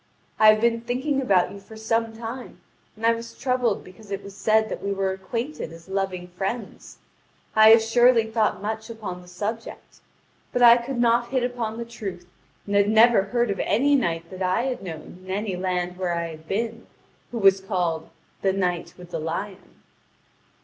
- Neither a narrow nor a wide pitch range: Yes, average, 3.9 semitones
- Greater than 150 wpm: Yes, average, 190 wpm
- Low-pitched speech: No, high, 215 Hz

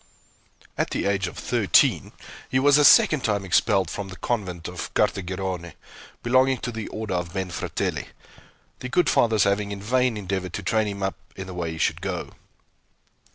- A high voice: No, low, 100 Hz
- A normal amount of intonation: Yes, average, 3.8 semitones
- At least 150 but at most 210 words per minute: Yes, average, 175 wpm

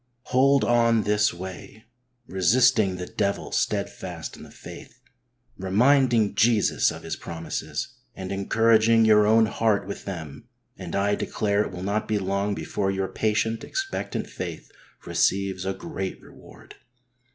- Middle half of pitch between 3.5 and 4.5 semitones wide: No, average, 2.9 semitones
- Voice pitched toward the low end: Yes, low, 105 Hz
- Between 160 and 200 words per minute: No, average, 140 wpm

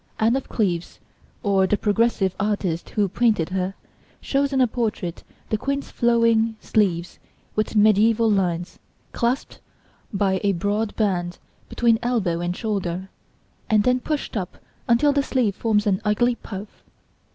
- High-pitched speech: Yes, high, 210 Hz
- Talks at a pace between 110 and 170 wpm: Yes, average, 140 wpm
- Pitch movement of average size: Yes, average, 3.6 semitones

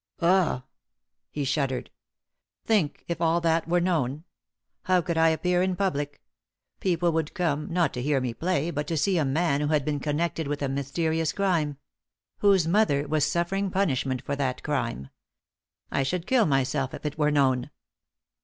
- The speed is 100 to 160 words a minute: No, average, 170 wpm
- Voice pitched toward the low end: No, medium, 155 Hz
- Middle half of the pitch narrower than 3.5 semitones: No, average, 3.8 semitones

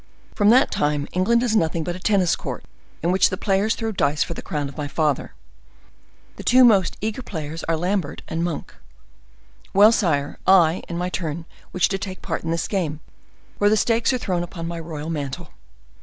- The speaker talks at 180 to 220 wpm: Yes, average, 200 wpm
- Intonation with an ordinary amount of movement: Yes, average, 4.3 semitones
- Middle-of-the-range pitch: Yes, medium, 175 Hz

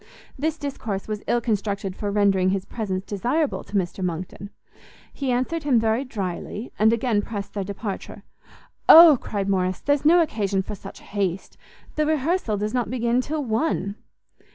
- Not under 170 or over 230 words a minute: No, average, 160 wpm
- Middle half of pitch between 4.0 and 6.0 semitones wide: Yes, average, 4.7 semitones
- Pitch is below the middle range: No, high, 215 Hz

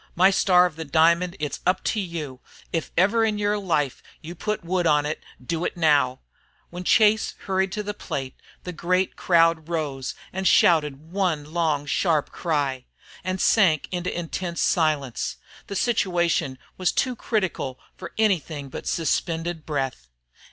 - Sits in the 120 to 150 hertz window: No, medium, 170 Hz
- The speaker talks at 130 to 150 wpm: No, average, 160 wpm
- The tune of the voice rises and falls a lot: No, average, 3.7 semitones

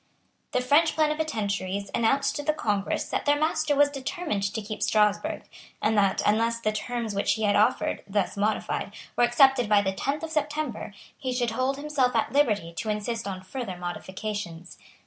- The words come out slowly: No, average, 175 wpm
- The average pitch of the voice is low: No, high, 230 Hz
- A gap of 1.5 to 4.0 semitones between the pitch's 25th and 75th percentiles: No, wide, 5.5 semitones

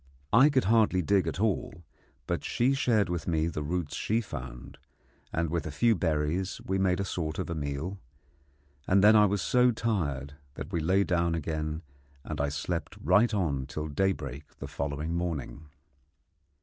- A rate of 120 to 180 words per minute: Yes, average, 175 wpm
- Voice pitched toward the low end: Yes, very low, 85 Hz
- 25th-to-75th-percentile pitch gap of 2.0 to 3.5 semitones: No, average, 4.5 semitones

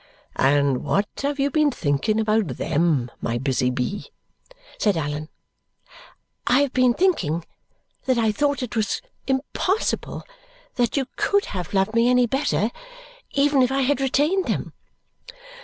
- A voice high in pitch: Yes, high, 230 Hz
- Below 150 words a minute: Yes, average, 140 wpm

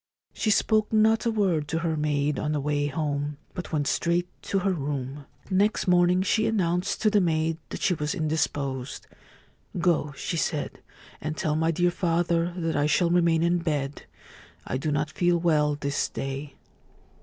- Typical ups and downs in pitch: Yes, average, 3.2 semitones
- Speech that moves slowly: No, average, 180 wpm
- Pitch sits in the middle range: Yes, medium, 160 Hz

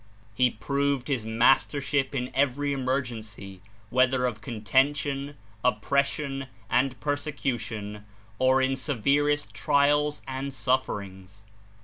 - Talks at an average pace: No, slow, 100 wpm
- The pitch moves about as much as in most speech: Yes, average, 3.2 semitones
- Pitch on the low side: Yes, low, 130 Hz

